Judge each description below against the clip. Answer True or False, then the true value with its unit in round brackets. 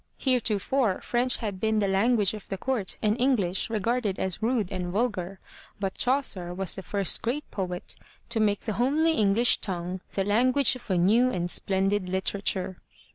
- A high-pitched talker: True (205 Hz)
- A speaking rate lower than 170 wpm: False (175 wpm)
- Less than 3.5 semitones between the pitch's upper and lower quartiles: False (4.2 semitones)